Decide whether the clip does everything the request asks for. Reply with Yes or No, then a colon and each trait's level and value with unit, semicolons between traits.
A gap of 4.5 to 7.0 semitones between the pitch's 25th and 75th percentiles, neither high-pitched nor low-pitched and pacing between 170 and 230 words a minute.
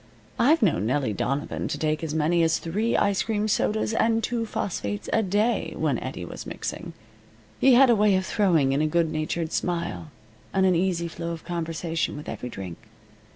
Yes: average, 5.2 semitones; medium, 170 Hz; average, 190 wpm